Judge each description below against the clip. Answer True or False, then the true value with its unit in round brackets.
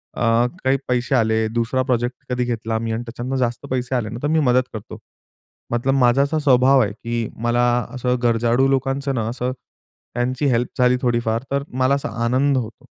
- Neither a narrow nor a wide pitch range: False (2.0 semitones)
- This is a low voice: True (125 Hz)